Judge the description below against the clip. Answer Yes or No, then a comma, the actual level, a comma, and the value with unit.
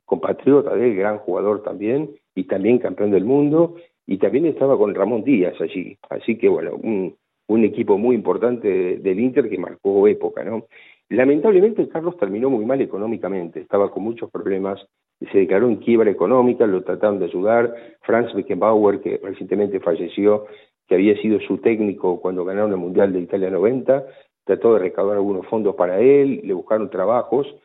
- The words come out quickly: No, average, 165 wpm